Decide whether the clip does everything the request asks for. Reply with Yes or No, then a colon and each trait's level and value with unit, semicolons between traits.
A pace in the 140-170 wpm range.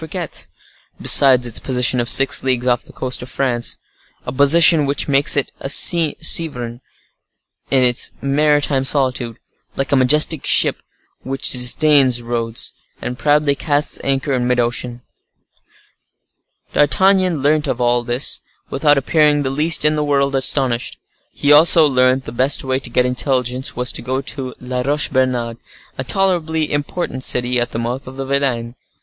Yes: average, 155 wpm